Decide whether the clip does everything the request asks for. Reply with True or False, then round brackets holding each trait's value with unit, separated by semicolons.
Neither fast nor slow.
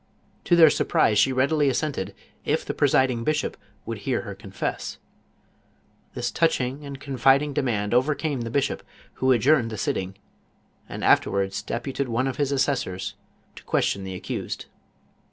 True (155 wpm)